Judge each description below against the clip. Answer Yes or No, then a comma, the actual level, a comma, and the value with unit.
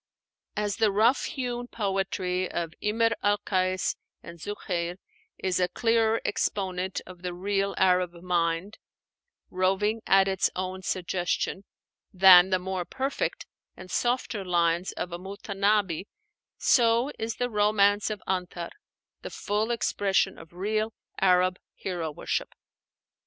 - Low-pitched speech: No, high, 190 Hz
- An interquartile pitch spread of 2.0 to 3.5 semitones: Yes, narrow, 2.6 semitones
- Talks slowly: Yes, slow, 125 wpm